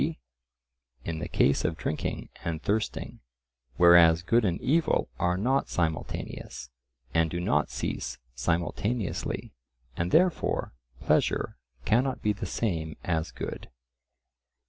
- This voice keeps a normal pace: No, slow, 120 wpm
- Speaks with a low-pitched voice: Yes, very low, 85 Hz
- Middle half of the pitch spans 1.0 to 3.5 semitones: No, average, 5.2 semitones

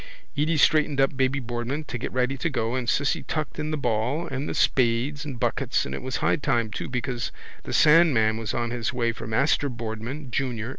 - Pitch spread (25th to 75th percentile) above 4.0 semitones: No, average, 3.6 semitones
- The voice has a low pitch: Yes, low, 130 Hz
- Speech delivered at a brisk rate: Yes, fast, 210 wpm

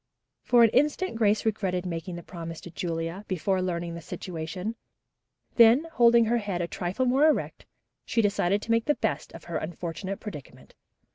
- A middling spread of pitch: Yes, average, 5.0 semitones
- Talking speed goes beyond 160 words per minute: Yes, average, 170 wpm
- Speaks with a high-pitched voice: Yes, high, 195 Hz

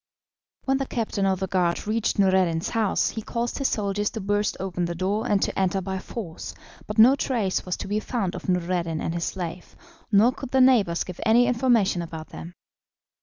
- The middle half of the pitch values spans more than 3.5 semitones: Yes, average, 4.1 semitones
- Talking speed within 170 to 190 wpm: No, average, 200 wpm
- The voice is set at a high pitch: Yes, high, 195 Hz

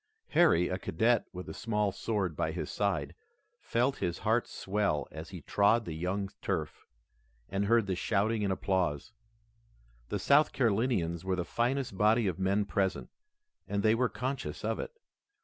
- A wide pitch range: No, average, 3.8 semitones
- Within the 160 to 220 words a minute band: Yes, average, 165 wpm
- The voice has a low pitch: Yes, low, 100 Hz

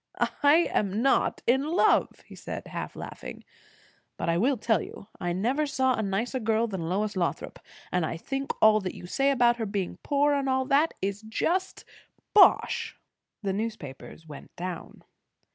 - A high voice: Yes, high, 220 Hz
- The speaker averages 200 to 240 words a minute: No, average, 170 wpm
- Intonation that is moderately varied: No, wide, 6.1 semitones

